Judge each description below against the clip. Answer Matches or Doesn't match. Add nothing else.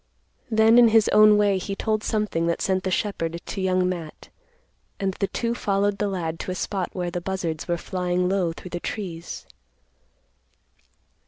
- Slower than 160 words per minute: Doesn't match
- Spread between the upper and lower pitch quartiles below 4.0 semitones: Matches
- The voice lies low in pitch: Doesn't match